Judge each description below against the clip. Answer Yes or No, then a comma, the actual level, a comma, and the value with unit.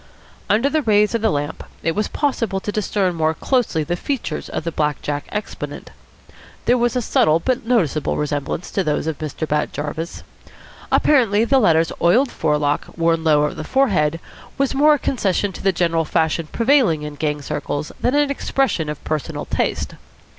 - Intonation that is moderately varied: No, wide, 7.6 semitones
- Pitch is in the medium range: Yes, medium, 170 Hz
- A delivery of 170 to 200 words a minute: Yes, average, 180 wpm